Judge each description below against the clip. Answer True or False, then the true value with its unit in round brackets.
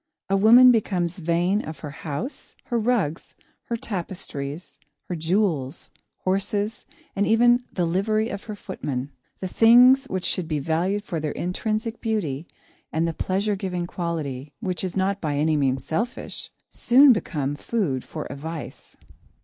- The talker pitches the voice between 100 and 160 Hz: False (185 Hz)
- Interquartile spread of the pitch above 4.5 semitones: True (5.4 semitones)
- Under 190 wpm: True (155 wpm)